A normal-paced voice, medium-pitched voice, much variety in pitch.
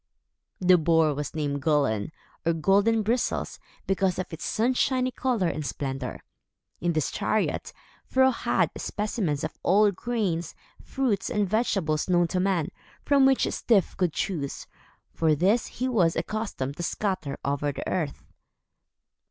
Yes: average, 145 wpm; medium, 180 Hz; wide, 5.9 semitones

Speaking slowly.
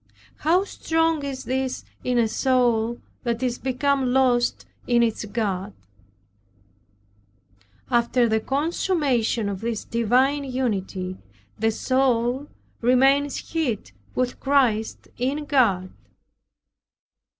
Yes: slow, 100 wpm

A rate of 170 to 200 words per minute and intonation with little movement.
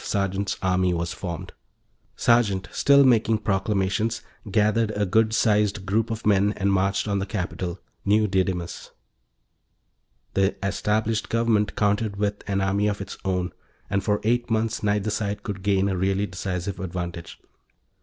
No: average, 145 wpm; narrow, 2.1 semitones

